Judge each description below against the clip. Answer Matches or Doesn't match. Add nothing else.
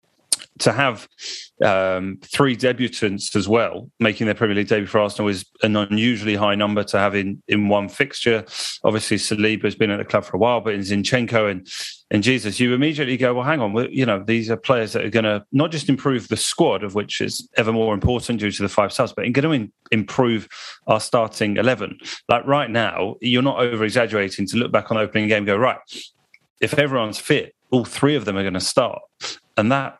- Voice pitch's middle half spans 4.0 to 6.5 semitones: Doesn't match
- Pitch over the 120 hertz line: Doesn't match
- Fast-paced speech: Matches